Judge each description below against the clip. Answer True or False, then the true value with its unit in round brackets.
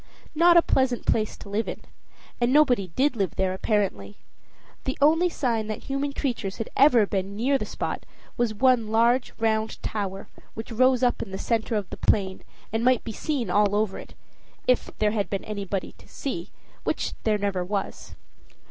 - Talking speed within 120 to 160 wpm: False (185 wpm)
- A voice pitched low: False (220 Hz)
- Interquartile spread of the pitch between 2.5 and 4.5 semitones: True (4.2 semitones)